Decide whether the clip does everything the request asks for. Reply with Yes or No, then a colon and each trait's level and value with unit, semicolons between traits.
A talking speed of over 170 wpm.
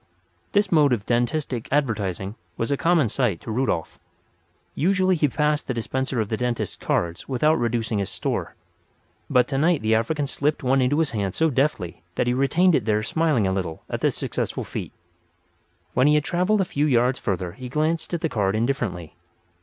Yes: average, 185 wpm